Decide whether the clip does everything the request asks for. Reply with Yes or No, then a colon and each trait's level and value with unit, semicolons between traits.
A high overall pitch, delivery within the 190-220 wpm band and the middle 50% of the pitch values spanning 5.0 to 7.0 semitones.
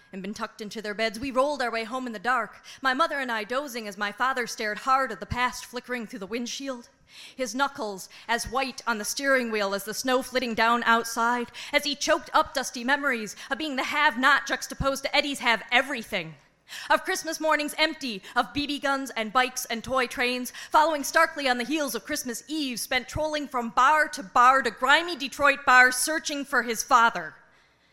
No: very high, 255 Hz; fast, 205 wpm; average, 3.5 semitones